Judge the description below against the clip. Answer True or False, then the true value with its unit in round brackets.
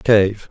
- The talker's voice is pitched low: True (105 Hz)